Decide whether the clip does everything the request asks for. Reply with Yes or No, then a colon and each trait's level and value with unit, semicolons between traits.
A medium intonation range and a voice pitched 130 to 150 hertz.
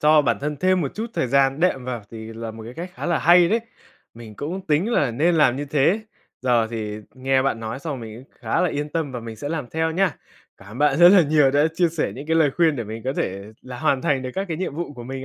Yes: average, 5.0 semitones; medium, 140 Hz